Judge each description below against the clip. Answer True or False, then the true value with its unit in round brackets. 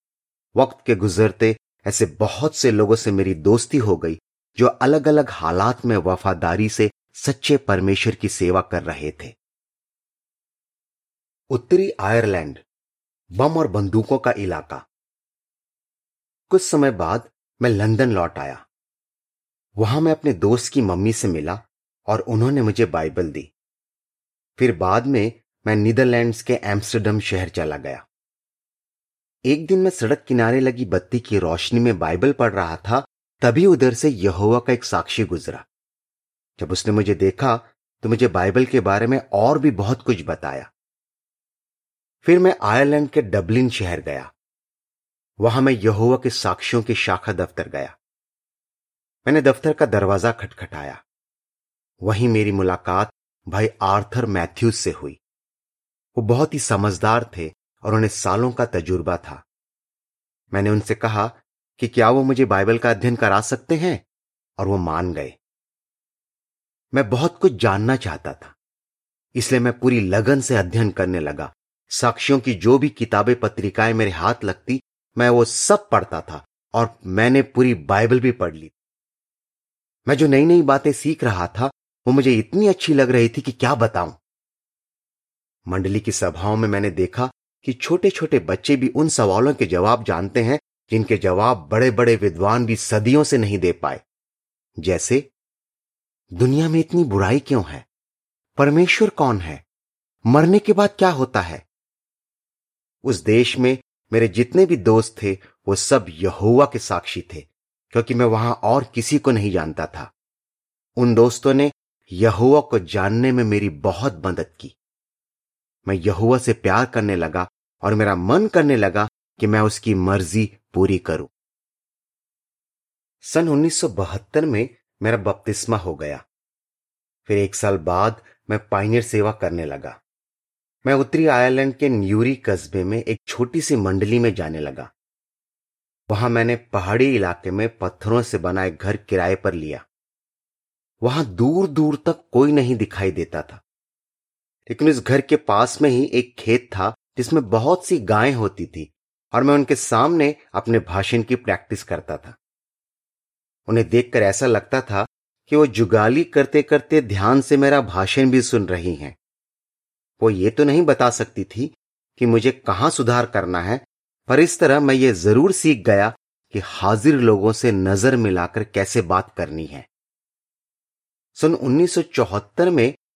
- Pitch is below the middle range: True (115 Hz)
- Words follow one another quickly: False (150 wpm)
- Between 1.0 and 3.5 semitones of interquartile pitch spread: False (5.0 semitones)